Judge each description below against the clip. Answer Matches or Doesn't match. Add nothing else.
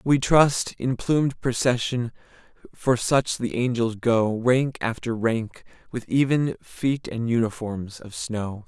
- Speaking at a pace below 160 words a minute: Matches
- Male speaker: Matches